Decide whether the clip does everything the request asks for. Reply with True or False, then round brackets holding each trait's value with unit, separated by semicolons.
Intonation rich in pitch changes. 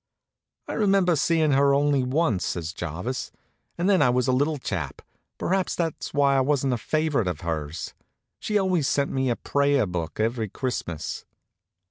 True (6.2 semitones)